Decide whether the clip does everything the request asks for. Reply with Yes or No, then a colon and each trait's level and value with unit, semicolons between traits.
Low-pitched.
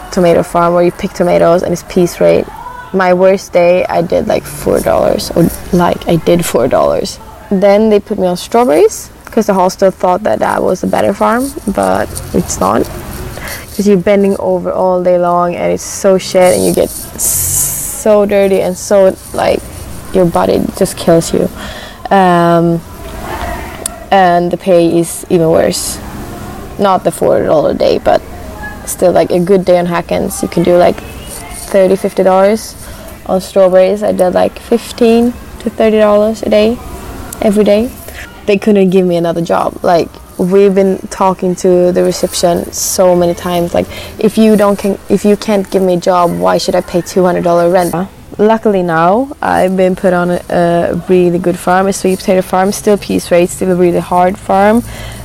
No: medium, 185 Hz